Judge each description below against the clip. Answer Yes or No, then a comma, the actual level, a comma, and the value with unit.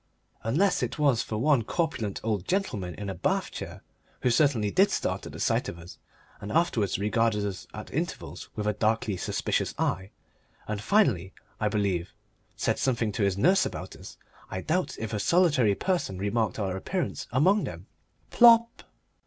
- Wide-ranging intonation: Yes, wide, 7.6 semitones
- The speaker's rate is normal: Yes, average, 175 wpm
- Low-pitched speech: Yes, low, 110 Hz